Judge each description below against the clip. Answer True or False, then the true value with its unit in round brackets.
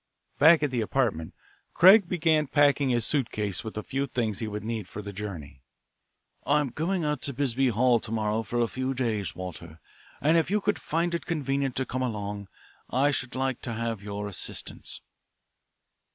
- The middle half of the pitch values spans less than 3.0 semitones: False (5.4 semitones)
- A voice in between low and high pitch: False (125 Hz)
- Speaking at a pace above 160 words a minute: True (180 wpm)